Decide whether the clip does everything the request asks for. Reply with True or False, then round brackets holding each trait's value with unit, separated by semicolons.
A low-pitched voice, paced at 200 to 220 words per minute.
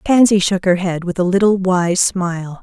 False (185 Hz; 205 wpm)